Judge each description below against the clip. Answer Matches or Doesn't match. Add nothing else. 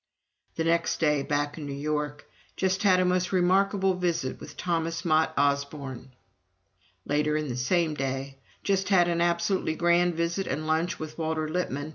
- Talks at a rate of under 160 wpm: Doesn't match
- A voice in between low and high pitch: Matches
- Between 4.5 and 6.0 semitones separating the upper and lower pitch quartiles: Doesn't match